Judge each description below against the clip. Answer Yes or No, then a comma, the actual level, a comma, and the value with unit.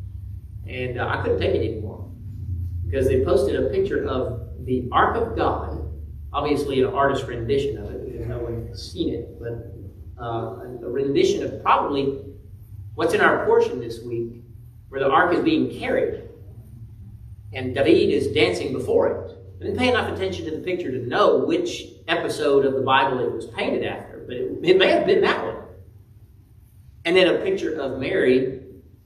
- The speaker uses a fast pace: No, average, 175 wpm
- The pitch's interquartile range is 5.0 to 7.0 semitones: Yes, wide, 5.4 semitones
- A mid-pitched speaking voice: No, low, 115 Hz